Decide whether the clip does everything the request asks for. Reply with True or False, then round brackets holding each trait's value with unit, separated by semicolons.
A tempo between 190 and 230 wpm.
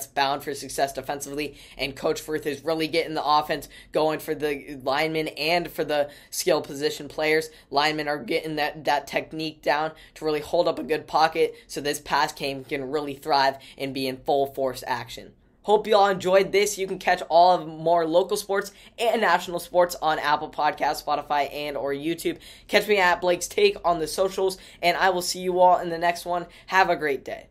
True (205 wpm)